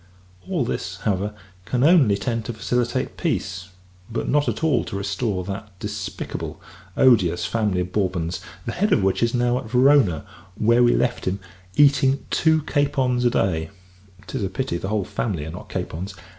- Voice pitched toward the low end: Yes, low, 105 Hz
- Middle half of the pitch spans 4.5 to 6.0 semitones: Yes, average, 5.1 semitones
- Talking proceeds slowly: No, average, 170 wpm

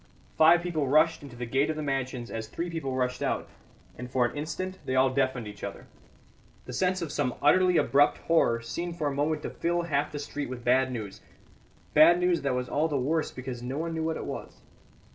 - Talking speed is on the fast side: Yes, fast, 220 wpm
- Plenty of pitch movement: No, average, 4.3 semitones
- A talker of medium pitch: Yes, medium, 145 Hz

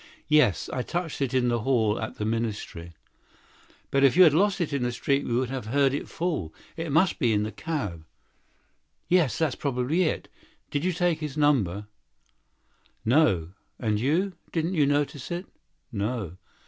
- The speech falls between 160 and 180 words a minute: Yes, average, 165 wpm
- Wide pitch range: Yes, wide, 6.2 semitones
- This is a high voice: No, low, 135 Hz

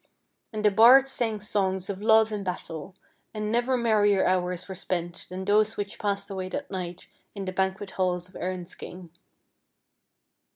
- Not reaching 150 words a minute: No, average, 165 wpm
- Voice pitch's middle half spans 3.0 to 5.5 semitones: No, narrow, 2.6 semitones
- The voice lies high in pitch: Yes, high, 195 Hz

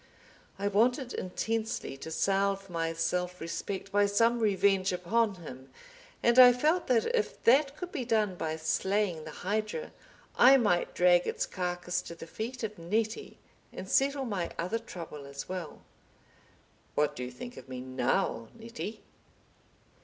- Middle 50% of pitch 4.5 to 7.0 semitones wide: Yes, average, 5.3 semitones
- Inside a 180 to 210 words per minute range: No, average, 155 wpm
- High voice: Yes, high, 195 Hz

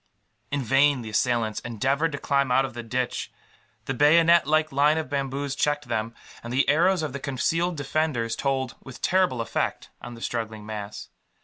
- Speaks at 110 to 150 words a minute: No, average, 180 wpm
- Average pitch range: Yes, average, 3.7 semitones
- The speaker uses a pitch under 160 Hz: Yes, low, 135 Hz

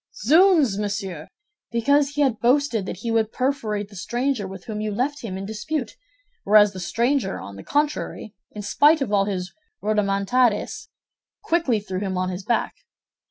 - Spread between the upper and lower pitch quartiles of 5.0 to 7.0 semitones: Yes, wide, 5.5 semitones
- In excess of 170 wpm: No, average, 165 wpm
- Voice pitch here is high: Yes, high, 215 Hz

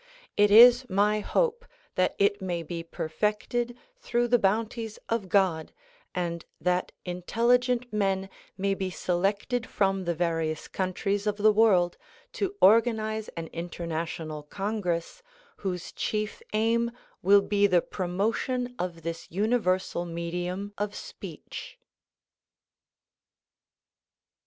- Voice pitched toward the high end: Yes, high, 200 Hz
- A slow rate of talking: Yes, slow, 115 wpm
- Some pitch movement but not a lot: Yes, average, 3.9 semitones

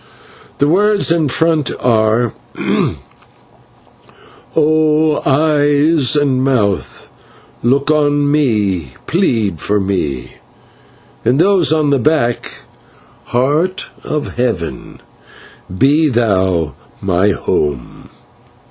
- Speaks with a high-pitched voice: No, medium, 140 Hz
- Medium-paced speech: No, slow, 85 wpm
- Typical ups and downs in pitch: No, wide, 6.7 semitones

